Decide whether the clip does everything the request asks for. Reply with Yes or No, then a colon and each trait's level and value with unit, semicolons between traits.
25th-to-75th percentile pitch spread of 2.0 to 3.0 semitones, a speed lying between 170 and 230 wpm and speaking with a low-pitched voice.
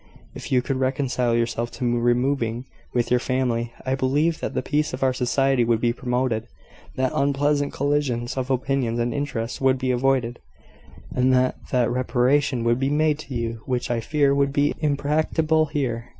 Yes: average, 2.7 semitones; average, 175 wpm; low, 130 Hz